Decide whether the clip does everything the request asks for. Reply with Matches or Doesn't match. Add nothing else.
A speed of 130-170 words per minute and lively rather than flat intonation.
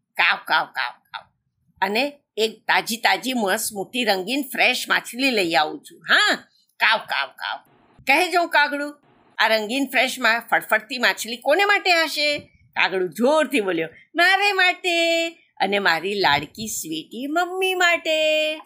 Matches